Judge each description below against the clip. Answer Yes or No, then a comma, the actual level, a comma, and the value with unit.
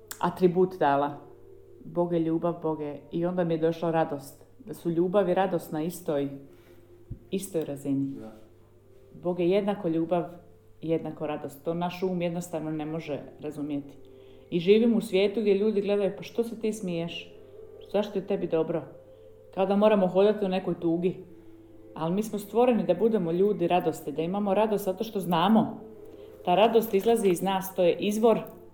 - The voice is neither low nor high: Yes, medium, 175 Hz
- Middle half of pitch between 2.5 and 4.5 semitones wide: No, average, 5.0 semitones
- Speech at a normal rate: No, fast, 165 wpm